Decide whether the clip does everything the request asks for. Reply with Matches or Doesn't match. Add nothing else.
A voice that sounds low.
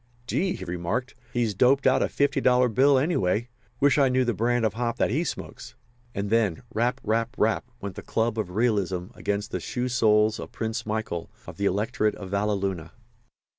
Matches